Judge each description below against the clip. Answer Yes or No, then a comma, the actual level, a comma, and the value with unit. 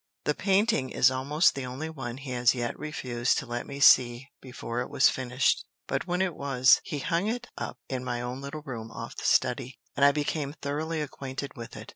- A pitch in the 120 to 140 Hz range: Yes, low, 135 Hz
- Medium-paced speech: No, fast, 210 wpm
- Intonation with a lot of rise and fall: No, average, 3.2 semitones